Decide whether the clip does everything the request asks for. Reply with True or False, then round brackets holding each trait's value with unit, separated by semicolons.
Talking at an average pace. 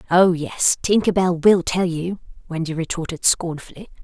True (150 wpm)